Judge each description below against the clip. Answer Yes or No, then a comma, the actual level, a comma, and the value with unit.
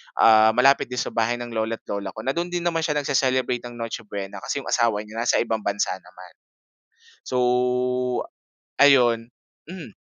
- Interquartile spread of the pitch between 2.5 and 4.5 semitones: Yes, average, 3.4 semitones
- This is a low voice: Yes, low, 120 Hz